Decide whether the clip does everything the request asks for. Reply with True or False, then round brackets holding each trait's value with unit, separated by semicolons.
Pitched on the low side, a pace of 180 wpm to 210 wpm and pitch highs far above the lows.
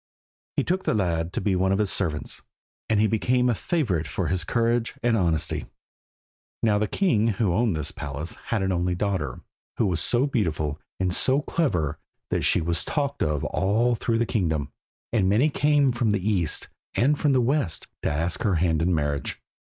True (100 Hz; 190 wpm; 6.2 semitones)